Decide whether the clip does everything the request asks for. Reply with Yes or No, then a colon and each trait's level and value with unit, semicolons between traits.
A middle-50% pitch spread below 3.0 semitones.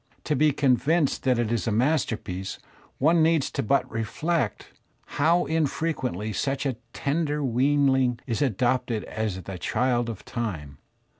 No: average, 4.7 semitones